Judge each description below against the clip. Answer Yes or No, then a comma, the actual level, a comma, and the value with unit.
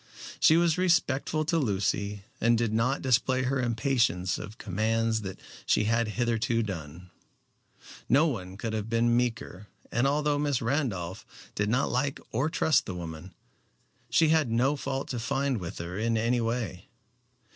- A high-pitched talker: No, low, 115 Hz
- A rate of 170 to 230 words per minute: No, average, 155 wpm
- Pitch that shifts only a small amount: No, average, 4.6 semitones